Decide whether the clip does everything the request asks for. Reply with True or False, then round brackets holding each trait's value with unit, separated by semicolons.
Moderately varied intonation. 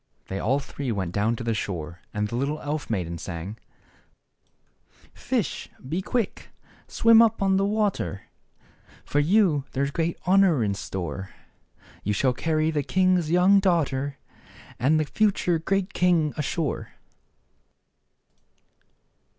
False (8.7 semitones)